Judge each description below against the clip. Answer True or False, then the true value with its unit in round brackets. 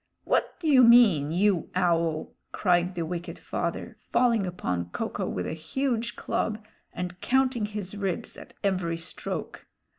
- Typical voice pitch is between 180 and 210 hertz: True (185 Hz)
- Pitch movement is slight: False (5.1 semitones)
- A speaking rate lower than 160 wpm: True (150 wpm)